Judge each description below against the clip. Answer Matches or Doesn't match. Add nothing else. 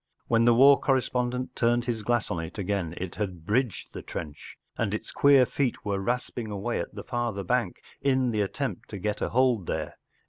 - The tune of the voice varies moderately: Matches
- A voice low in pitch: Matches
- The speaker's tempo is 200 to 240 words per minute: Matches